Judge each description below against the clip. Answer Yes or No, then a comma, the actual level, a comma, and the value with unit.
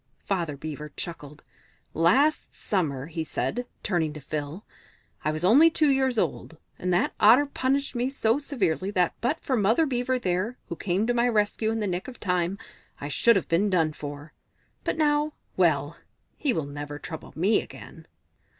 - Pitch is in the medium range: No, high, 195 Hz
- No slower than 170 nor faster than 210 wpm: Yes, average, 175 wpm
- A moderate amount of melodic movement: No, wide, 7.5 semitones